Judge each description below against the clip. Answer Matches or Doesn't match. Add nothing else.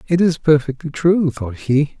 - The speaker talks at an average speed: Matches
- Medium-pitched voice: Matches